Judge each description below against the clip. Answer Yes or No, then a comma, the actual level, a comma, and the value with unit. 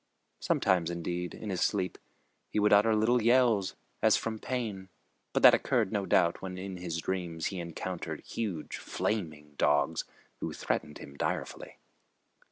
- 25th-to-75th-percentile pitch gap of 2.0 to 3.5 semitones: No, average, 3.9 semitones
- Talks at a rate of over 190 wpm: No, average, 150 wpm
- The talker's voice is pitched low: Yes, very low, 95 Hz